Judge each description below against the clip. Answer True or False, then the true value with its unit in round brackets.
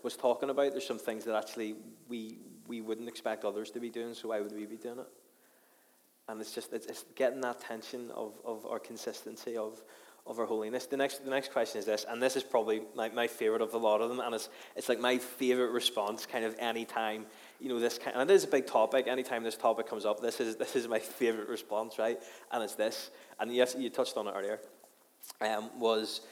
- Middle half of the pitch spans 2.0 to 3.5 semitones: True (2.4 semitones)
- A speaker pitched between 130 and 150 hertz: False (115 Hz)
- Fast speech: True (235 wpm)